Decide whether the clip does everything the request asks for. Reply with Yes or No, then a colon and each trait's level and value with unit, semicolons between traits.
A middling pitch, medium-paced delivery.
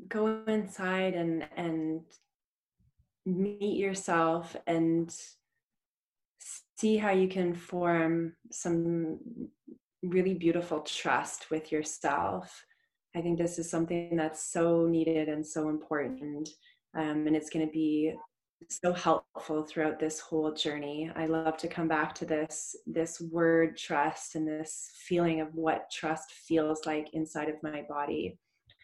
No: medium, 165 Hz; slow, 130 wpm